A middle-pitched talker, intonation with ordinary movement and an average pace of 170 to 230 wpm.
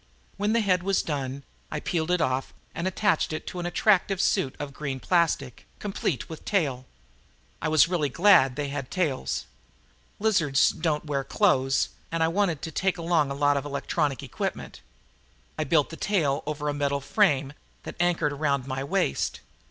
Yes: medium, 155 Hz; average, 4.2 semitones; average, 175 wpm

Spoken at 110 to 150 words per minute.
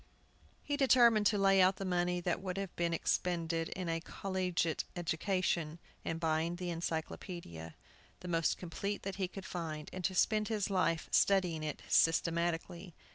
No: average, 160 wpm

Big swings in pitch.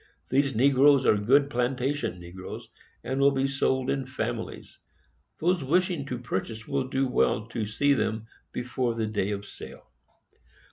No: average, 3.7 semitones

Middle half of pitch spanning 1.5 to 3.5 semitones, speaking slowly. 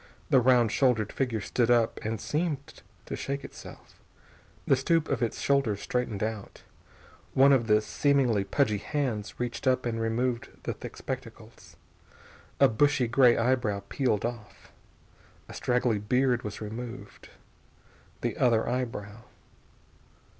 Yes: average, 2.9 semitones; slow, 130 wpm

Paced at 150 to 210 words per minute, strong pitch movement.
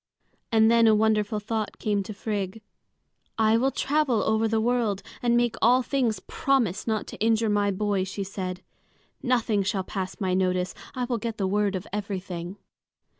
No: average, 175 wpm; average, 2.8 semitones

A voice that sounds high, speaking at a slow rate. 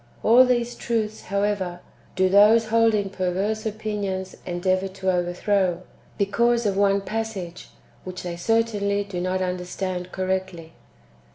Yes: high, 195 Hz; slow, 125 wpm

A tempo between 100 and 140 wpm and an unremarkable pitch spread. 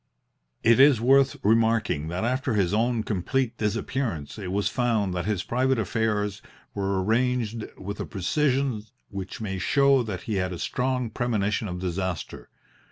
No: average, 155 wpm; average, 4.3 semitones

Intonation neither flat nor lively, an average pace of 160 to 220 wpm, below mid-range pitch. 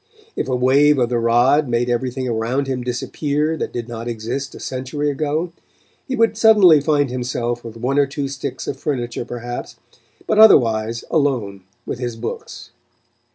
Yes: average, 3.3 semitones; average, 165 wpm; low, 130 Hz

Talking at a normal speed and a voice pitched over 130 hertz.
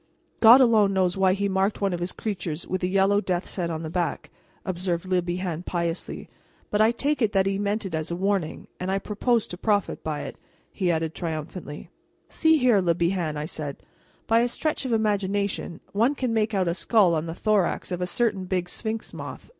No: fast, 210 wpm; high, 190 Hz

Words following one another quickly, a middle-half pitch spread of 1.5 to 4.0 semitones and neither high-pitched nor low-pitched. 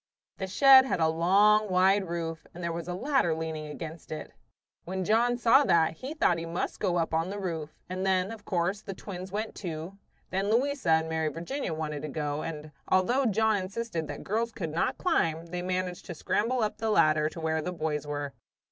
No: fast, 210 wpm; average, 4.6 semitones; medium, 180 Hz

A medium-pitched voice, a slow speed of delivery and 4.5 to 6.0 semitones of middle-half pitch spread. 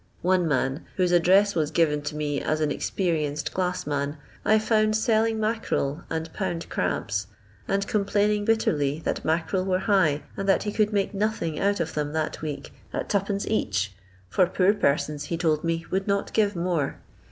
No: medium, 180 Hz; average, 175 wpm; average, 4.9 semitones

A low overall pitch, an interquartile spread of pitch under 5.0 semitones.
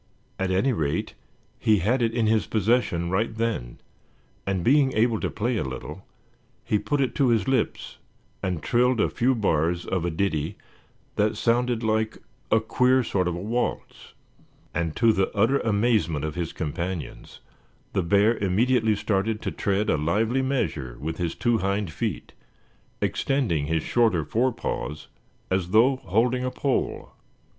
No: low, 105 Hz; average, 5.3 semitones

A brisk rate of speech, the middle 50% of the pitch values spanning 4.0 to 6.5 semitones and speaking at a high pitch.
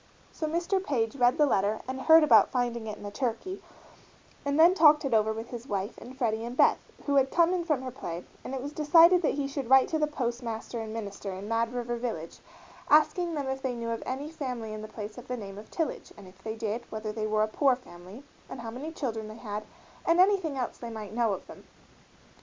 Yes: fast, 240 wpm; average, 4.8 semitones; high, 245 Hz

